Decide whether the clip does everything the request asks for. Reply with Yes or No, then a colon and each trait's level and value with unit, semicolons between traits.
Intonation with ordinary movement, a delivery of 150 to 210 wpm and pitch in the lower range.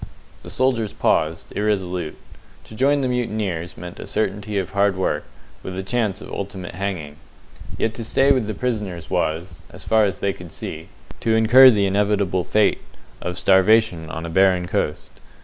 Yes: average, 3.6 semitones; average, 170 wpm; low, 100 Hz